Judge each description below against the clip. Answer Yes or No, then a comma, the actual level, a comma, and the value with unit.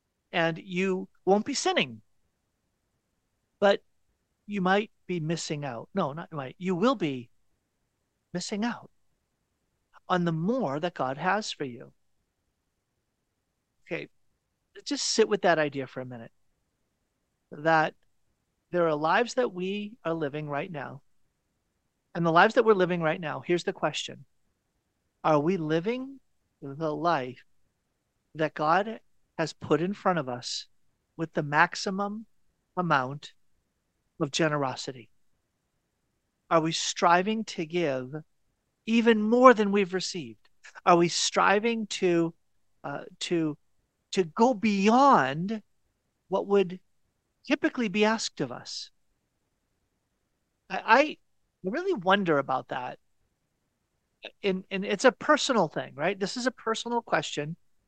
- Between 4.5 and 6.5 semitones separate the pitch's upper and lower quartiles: Yes, wide, 5.6 semitones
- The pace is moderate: No, slow, 125 wpm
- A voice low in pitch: No, medium, 175 Hz